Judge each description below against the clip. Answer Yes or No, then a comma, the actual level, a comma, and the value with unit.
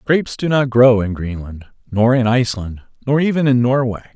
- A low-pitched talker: Yes, low, 120 Hz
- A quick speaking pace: No, average, 190 wpm